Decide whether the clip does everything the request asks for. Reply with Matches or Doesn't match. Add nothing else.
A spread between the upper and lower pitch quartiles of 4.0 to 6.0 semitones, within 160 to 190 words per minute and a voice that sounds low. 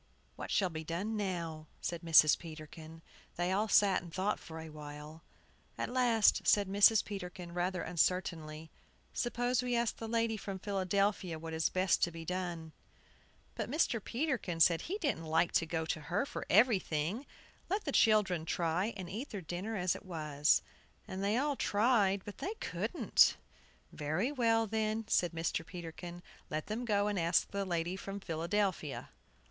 Doesn't match